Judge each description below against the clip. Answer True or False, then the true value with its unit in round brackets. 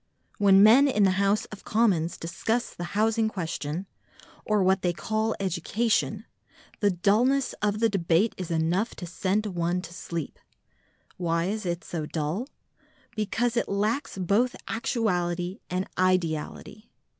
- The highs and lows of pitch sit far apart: False (3.8 semitones)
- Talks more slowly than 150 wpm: True (140 wpm)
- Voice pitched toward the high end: True (195 Hz)